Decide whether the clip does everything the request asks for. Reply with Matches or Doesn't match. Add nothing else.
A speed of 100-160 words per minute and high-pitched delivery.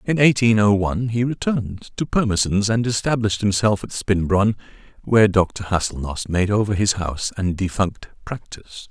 Doesn't match